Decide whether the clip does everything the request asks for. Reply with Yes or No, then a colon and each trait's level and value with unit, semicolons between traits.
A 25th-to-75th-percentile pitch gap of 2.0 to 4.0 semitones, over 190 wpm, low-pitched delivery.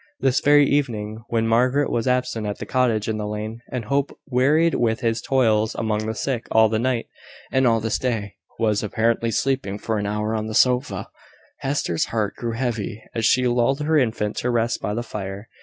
Yes: average, 2.8 semitones; average, 200 wpm; low, 115 Hz